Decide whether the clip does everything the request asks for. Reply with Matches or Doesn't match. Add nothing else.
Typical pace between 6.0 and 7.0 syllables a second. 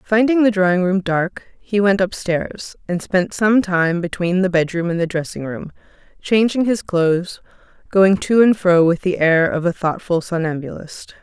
Doesn't match